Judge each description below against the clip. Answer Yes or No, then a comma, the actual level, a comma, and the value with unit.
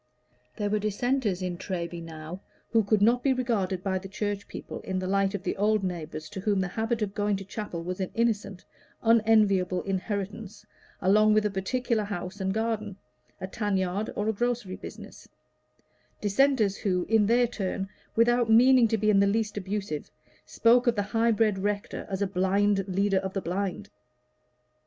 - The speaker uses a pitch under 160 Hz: No, high, 205 Hz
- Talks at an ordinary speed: Yes, average, 180 wpm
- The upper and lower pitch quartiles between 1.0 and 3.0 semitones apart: Yes, average, 2.7 semitones